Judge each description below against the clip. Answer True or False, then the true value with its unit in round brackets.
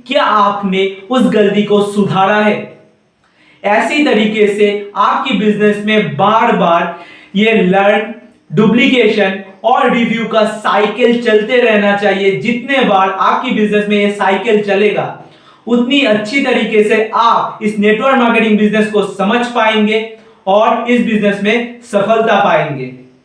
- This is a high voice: True (215 Hz)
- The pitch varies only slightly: True (2.2 semitones)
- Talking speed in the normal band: True (130 wpm)